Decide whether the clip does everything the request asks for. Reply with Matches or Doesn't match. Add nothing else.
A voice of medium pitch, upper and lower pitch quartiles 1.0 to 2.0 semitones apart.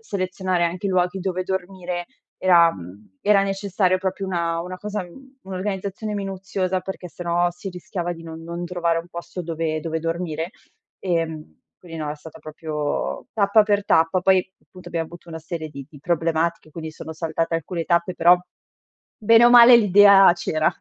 Doesn't match